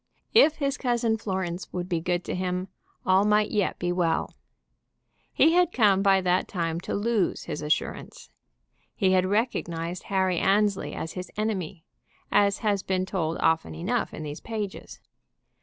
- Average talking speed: Yes, average, 155 wpm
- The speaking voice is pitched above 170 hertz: Yes, high, 190 Hz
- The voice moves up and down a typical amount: Yes, average, 3.1 semitones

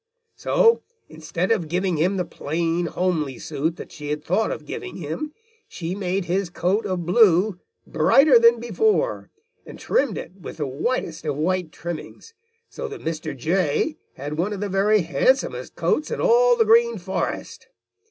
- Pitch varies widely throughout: Yes, wide, 6.5 semitones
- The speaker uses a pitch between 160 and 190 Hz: Yes, medium, 185 Hz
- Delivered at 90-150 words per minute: No, average, 165 wpm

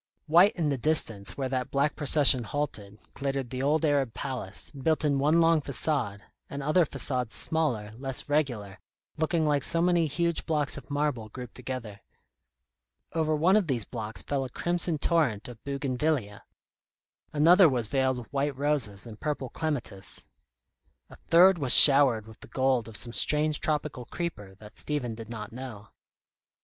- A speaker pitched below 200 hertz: Yes, medium, 140 Hz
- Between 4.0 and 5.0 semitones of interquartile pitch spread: Yes, average, 4.4 semitones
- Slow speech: No, average, 160 wpm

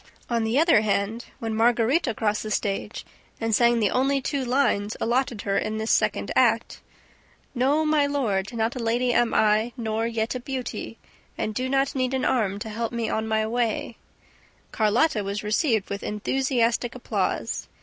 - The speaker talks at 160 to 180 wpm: Yes, average, 170 wpm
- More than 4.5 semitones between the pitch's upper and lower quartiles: No, average, 2.8 semitones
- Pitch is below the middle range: No, high, 230 Hz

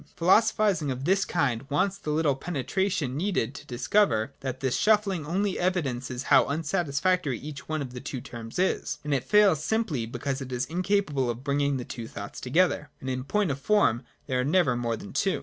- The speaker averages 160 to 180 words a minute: No, average, 200 wpm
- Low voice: No, medium, 145 Hz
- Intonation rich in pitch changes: Yes, wide, 6.3 semitones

